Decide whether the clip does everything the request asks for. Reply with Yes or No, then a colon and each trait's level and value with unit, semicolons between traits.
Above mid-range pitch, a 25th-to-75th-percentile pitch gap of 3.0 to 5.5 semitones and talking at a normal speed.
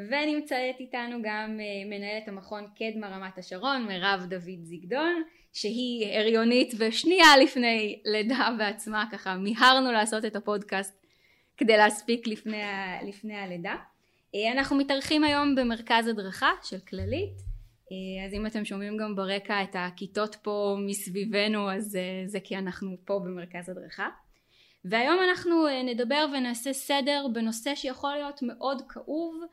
Yes: high, 215 Hz; average, 4.8 semitones; average, 125 wpm